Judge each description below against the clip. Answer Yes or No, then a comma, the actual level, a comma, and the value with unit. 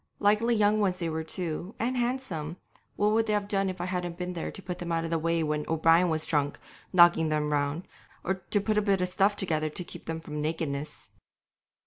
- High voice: No, medium, 175 Hz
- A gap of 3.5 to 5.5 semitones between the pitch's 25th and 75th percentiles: Yes, average, 3.9 semitones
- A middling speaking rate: No, fast, 235 wpm